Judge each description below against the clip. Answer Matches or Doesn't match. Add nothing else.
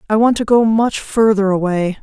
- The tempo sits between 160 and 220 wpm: Matches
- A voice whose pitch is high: Matches